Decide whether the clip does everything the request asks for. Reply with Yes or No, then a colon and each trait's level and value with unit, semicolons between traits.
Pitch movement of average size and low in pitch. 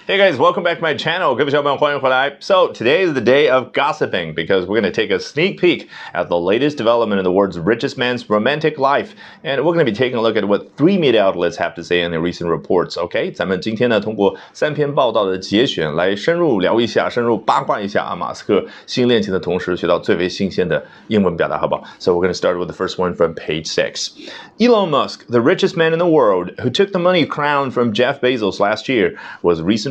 No: wide, 7.6 semitones; low, 125 Hz